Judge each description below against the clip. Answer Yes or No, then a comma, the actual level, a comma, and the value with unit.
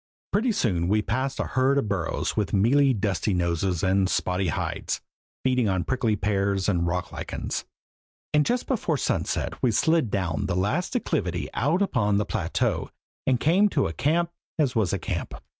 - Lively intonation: Yes, wide, 7.0 semitones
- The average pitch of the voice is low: Yes, low, 105 Hz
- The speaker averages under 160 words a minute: No, average, 175 wpm